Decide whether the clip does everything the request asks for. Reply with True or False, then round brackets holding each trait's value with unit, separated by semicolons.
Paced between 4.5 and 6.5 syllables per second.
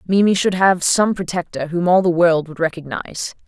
True (5.3 syllables/s)